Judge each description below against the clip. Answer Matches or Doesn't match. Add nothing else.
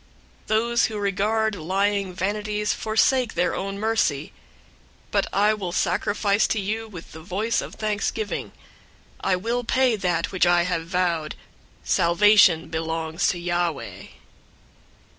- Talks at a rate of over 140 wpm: Doesn't match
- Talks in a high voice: Matches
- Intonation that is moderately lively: Matches